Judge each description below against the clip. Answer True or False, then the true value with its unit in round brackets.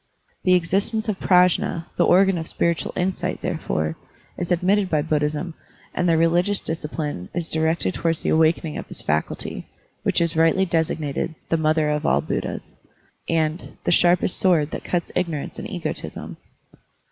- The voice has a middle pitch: True (165 Hz)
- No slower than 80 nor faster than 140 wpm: False (160 wpm)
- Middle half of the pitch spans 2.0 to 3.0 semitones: True (2.6 semitones)